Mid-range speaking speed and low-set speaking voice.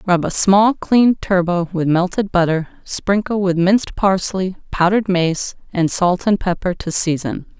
No: average, 160 wpm; medium, 185 Hz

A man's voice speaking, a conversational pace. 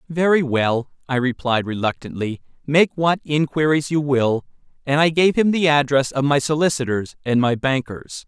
Yes: male; average, 160 wpm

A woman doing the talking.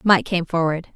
Yes: female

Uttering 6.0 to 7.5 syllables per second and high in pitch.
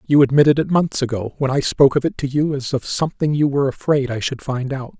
No: 6.2 syllables/s; low, 135 Hz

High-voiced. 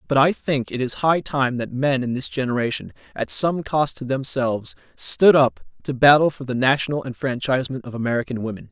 No: low, 135 Hz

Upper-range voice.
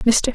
Yes: high, 230 Hz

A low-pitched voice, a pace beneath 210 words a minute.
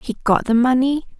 No: very high, 255 Hz; average, 200 wpm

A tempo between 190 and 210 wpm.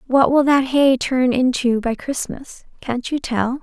No: average, 180 wpm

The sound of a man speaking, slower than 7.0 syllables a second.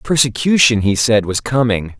Yes: male; 4.8 syllables/s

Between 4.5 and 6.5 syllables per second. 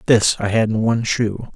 Yes: 5.3 syllables/s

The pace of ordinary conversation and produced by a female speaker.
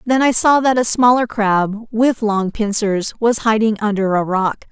Yes: average, 190 wpm; female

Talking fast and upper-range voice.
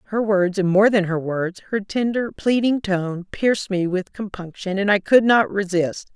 No: average, 195 wpm; high, 200 Hz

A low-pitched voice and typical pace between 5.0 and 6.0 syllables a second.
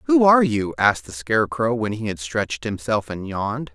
Yes: low, 120 Hz; 5.6 syllables/s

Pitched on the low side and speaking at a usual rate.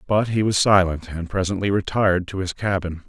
Yes: very low, 95 Hz; average, 195 wpm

